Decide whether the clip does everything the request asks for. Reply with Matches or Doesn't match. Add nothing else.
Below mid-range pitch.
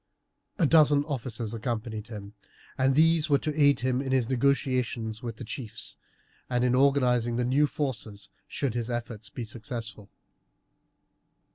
Matches